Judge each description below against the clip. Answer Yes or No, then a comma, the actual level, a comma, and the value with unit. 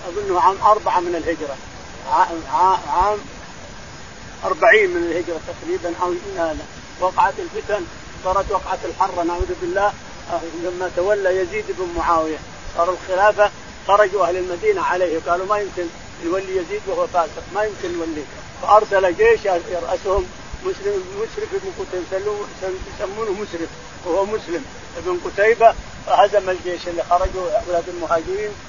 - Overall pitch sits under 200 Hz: Yes, medium, 185 Hz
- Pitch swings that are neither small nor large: Yes, average, 3.6 semitones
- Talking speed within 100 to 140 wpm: Yes, average, 125 wpm